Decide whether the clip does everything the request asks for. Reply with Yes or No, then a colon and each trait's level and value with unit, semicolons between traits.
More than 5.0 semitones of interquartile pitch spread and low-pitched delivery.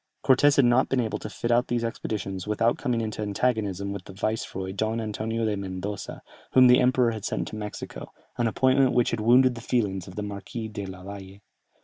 No: average, 3.3 semitones; low, 110 Hz